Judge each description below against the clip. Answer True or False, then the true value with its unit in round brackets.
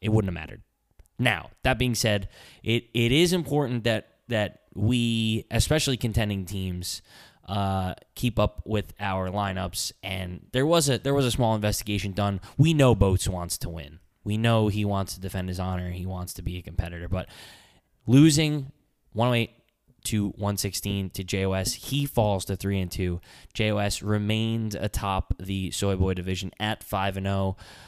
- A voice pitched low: True (100 Hz)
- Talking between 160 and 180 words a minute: True (170 wpm)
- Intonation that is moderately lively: True (3.6 semitones)